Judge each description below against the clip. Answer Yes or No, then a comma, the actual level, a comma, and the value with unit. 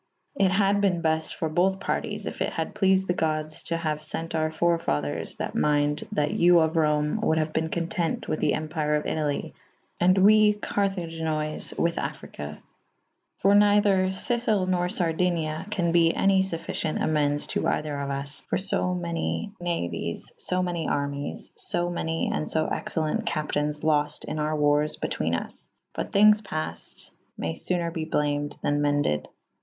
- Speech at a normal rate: Yes, average, 170 wpm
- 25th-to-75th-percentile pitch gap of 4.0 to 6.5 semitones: No, average, 3.3 semitones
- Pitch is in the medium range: Yes, medium, 160 Hz